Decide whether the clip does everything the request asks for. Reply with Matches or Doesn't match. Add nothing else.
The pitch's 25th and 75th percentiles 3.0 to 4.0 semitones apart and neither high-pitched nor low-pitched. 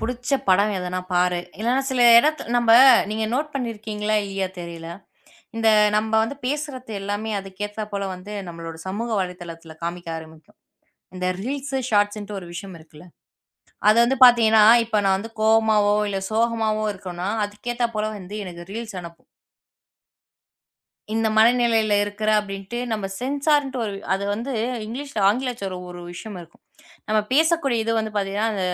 Doesn't match